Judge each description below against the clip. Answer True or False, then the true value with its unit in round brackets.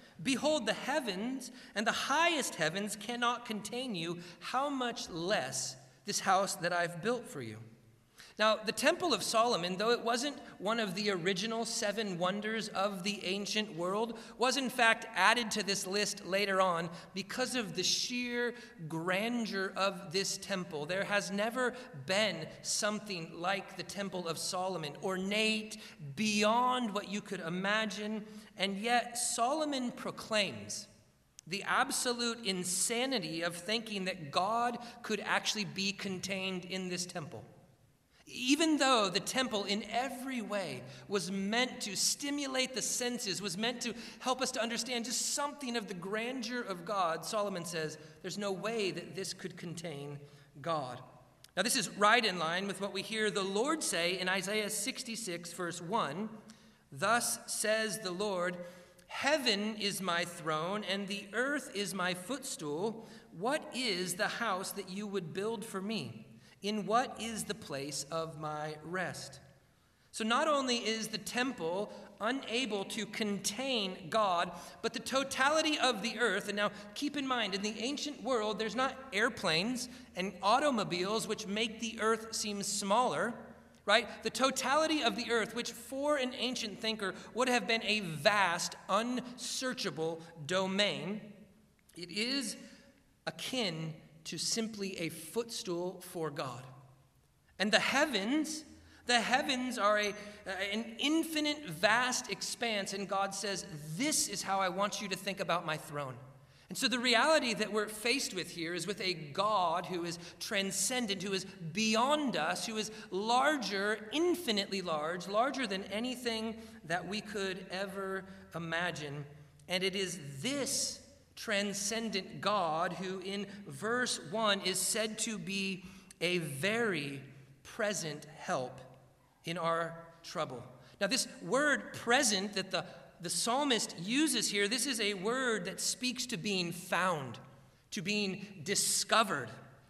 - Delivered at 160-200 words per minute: False (145 wpm)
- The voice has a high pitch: True (205 Hz)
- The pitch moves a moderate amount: True (4.4 semitones)